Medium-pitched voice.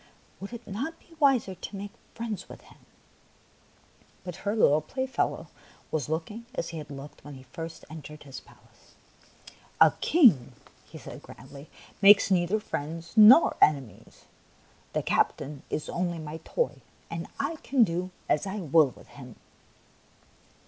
Yes: medium, 170 Hz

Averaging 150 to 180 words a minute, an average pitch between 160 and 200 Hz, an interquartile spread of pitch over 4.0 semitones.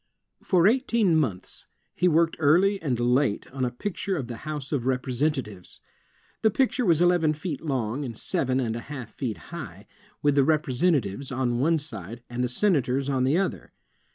No: average, 175 wpm; medium, 140 Hz; average, 5.1 semitones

